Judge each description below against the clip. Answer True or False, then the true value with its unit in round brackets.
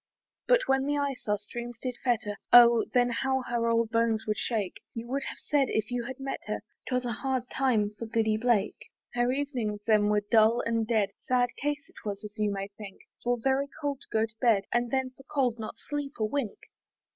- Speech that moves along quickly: True (215 wpm)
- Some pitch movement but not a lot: True (3.4 semitones)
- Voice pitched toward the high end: True (235 Hz)